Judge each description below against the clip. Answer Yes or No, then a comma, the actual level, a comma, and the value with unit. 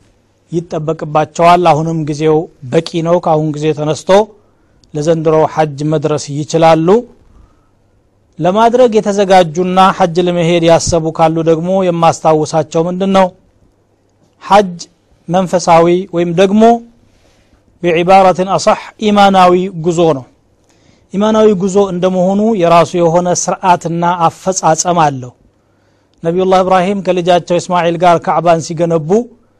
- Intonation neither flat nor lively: Yes, average, 3.4 semitones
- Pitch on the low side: No, medium, 170 Hz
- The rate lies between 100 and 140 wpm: No, average, 85 wpm